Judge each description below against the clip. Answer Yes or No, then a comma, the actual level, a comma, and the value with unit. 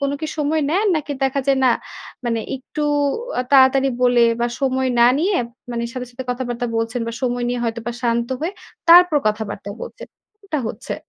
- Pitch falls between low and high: No, very high, 255 Hz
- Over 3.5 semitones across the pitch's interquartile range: No, average, 3.2 semitones